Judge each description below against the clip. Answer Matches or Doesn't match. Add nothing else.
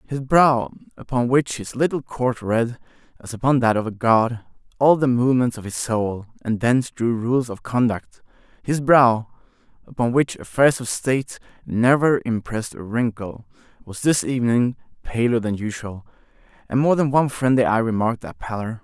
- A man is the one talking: Matches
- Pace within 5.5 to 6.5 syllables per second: Doesn't match